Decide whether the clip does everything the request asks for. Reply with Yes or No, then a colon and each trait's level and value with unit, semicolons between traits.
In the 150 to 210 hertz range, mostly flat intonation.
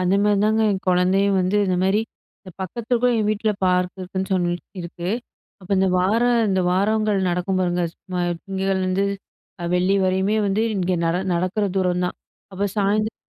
Yes: high, 190 Hz; narrow, 2.0 semitones